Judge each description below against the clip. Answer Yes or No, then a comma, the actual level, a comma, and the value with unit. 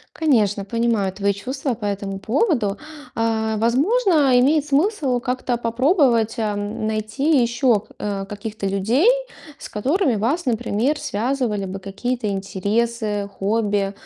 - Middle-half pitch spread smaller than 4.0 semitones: No, average, 4.3 semitones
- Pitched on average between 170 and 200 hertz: No, high, 230 Hz